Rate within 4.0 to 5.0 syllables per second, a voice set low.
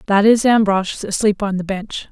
No: 4.7 syllables/s; high, 205 Hz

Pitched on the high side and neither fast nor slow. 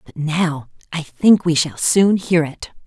No: medium, 160 Hz; average, 190 wpm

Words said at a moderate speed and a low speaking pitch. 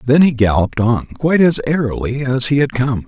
No: fast, 215 wpm; low, 130 Hz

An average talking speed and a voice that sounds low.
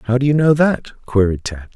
No: fast, 240 wpm; low, 125 Hz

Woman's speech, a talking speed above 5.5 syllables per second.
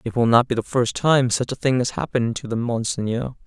No: male; 5.8 syllables/s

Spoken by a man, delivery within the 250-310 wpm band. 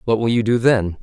Yes: male; fast, 290 wpm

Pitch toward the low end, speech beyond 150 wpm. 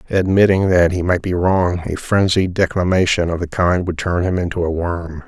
Yes: very low, 90 Hz; fast, 205 wpm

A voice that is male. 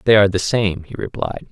Yes: male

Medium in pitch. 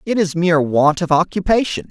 Yes: medium, 175 Hz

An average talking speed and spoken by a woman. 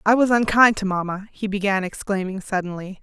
Yes: average, 180 wpm; female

